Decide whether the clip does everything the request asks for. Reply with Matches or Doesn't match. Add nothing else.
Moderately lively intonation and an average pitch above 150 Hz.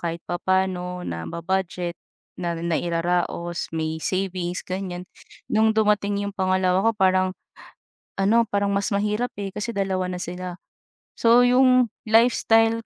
Matches